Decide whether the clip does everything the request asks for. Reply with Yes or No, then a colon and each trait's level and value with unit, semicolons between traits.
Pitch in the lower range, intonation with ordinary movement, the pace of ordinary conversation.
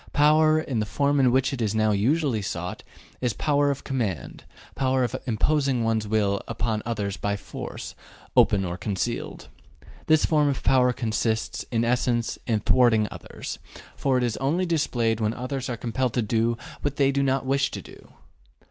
Yes: low, 125 Hz; average, 3.8 semitones; average, 175 wpm